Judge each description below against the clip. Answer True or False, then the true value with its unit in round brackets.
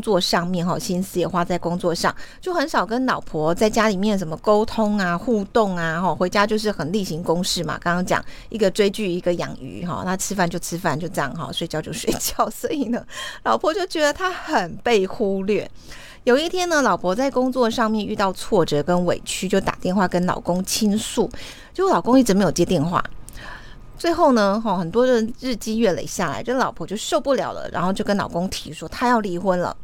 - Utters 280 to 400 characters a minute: True (310 characters per minute)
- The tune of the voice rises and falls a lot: False (4.9 semitones)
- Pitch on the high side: True (200 Hz)